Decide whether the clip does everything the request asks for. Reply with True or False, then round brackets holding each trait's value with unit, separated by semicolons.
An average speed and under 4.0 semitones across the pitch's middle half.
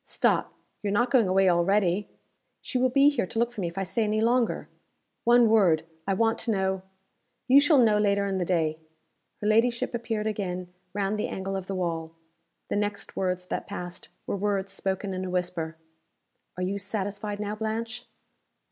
True (190 wpm; 3.3 semitones)